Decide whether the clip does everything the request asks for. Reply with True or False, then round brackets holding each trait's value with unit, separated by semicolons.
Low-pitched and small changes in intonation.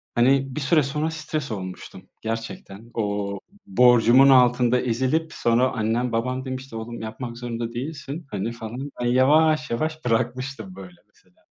False (125 Hz; 3.2 semitones)